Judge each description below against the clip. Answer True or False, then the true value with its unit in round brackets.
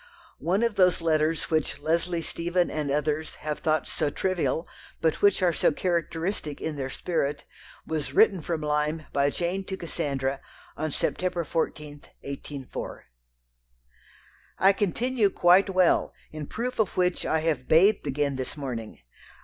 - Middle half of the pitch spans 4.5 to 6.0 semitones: False (3.5 semitones)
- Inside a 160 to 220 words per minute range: False (145 wpm)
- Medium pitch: True (160 Hz)